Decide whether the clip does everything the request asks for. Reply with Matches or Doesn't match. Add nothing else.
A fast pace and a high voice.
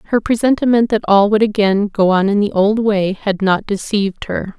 Matches